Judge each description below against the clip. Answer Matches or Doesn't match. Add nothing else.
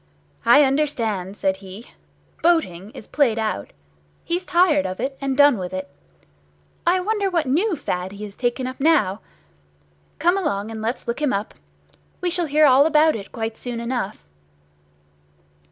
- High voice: Matches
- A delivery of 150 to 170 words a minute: Matches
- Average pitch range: Doesn't match